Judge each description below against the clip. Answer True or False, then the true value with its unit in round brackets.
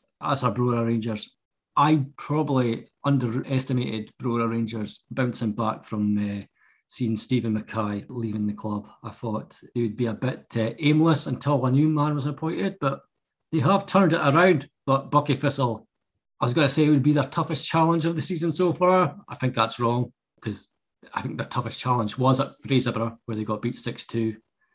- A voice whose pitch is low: True (130 Hz)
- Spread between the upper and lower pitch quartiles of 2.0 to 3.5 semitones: False (4.6 semitones)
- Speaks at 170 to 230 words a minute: True (185 wpm)